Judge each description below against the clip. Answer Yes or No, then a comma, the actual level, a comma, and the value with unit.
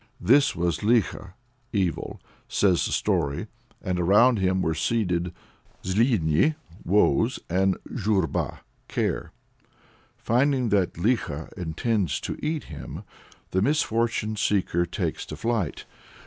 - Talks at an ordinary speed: No, slow, 110 wpm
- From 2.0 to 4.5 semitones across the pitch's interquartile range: No, average, 4.9 semitones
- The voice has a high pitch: No, low, 100 Hz